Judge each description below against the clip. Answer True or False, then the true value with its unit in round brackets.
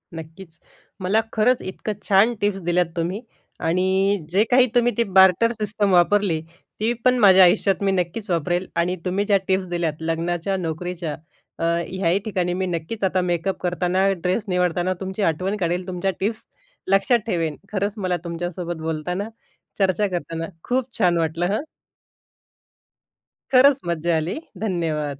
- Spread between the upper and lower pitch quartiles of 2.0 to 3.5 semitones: True (2.9 semitones)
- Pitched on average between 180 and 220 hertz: True (185 Hz)